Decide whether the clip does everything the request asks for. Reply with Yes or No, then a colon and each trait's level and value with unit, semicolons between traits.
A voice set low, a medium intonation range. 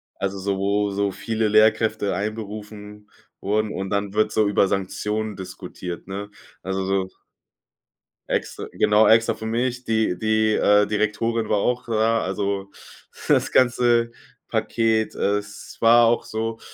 No: low, 105 Hz; narrow, 1.9 semitones